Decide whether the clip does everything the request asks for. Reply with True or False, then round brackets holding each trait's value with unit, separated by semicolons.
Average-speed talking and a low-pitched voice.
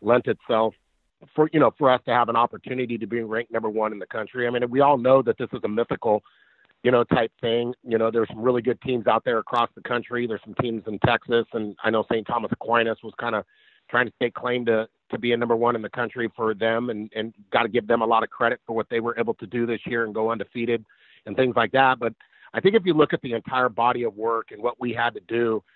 False (275 wpm; 115 Hz)